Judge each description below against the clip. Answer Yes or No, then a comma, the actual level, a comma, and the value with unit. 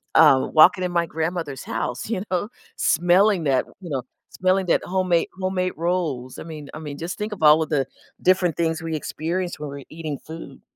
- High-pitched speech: No, medium, 165 Hz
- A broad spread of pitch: No, average, 3.4 semitones